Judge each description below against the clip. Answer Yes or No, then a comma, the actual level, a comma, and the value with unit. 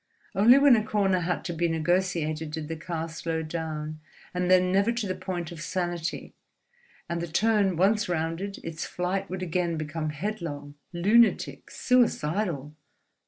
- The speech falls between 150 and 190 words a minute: Yes, average, 155 wpm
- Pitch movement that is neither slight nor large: Yes, average, 3.2 semitones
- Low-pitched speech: No, medium, 175 Hz